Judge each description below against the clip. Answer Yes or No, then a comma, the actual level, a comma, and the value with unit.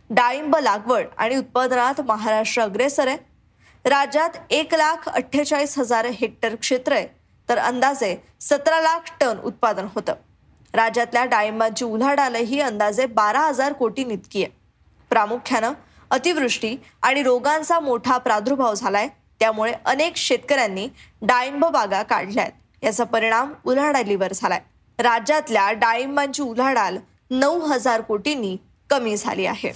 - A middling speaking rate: Yes, average, 115 wpm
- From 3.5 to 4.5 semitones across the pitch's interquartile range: Yes, average, 3.9 semitones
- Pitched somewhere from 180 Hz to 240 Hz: No, very high, 250 Hz